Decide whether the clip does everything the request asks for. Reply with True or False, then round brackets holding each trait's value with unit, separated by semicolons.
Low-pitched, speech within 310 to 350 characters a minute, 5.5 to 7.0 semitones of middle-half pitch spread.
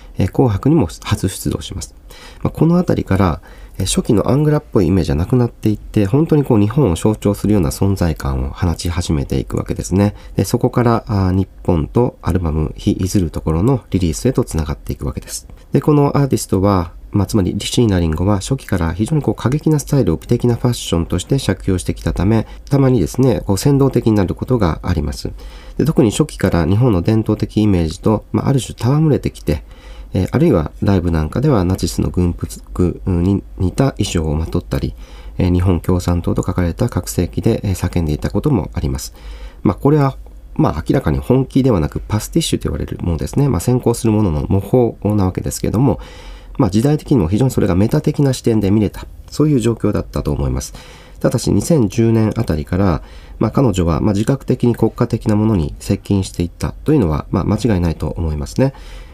False (100 Hz; 415 characters per minute; 6.0 semitones)